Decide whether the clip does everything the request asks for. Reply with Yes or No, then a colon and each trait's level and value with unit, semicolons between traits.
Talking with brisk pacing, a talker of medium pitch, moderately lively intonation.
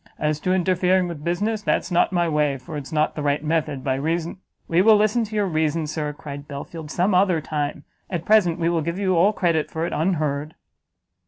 Yes: fast, 220 wpm; medium, 165 Hz; average, 3.5 semitones